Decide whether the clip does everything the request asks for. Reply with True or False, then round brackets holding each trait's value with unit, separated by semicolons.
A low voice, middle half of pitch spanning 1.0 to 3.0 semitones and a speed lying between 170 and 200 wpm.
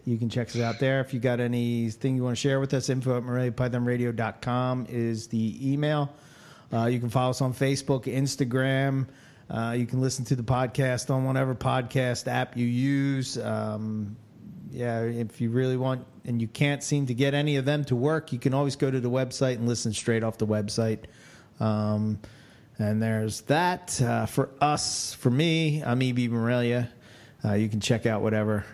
True (125 Hz; 2.7 semitones; 190 wpm)